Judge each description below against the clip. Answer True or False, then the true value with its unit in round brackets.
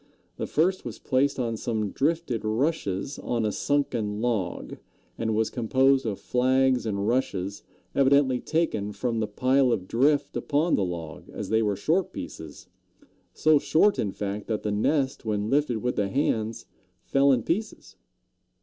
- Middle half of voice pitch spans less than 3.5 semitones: False (4.9 semitones)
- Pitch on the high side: False (120 Hz)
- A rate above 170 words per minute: False (160 wpm)